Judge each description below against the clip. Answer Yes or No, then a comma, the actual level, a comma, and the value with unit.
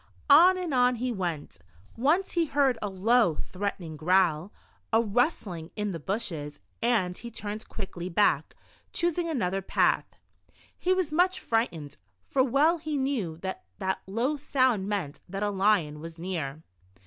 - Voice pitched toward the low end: No, high, 210 Hz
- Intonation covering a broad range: Yes, wide, 7.0 semitones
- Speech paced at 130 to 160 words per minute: Yes, average, 150 wpm